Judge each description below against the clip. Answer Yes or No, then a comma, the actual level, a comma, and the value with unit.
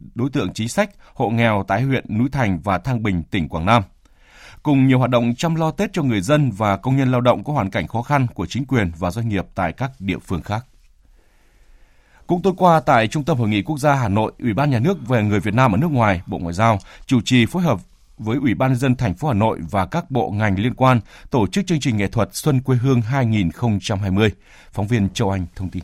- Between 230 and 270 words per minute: Yes, fast, 250 wpm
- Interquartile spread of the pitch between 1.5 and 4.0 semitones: No, average, 5.1 semitones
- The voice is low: Yes, low, 115 Hz